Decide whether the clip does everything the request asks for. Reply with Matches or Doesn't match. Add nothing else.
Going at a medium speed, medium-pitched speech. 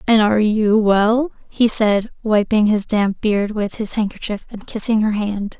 Doesn't match